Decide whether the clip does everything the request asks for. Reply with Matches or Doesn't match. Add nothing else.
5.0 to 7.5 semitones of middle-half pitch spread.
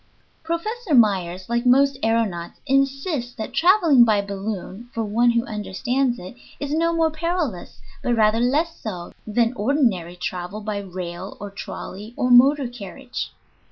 Matches